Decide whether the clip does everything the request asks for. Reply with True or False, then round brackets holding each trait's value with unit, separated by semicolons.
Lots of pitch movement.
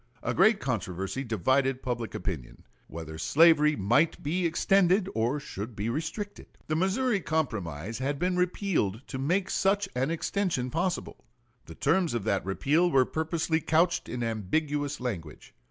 True (7.1 semitones)